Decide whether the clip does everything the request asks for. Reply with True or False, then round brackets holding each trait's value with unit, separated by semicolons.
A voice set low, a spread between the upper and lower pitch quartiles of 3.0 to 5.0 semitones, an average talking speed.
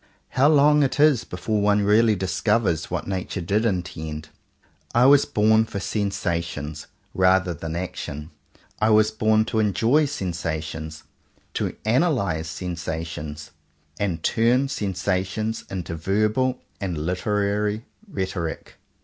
False (100 Hz; 4.6 semitones; 120 wpm)